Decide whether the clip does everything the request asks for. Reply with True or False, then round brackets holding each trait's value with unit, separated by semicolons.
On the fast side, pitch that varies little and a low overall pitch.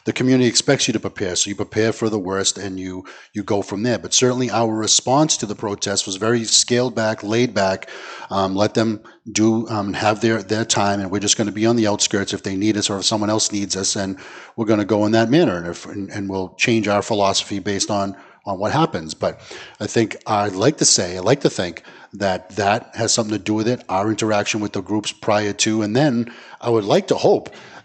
True (240 wpm; 2.1 semitones; 105 Hz)